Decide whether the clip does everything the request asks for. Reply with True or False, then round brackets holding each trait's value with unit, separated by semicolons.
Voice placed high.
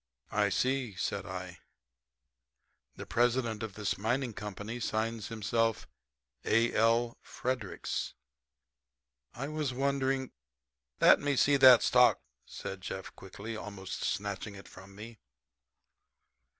False (115 Hz)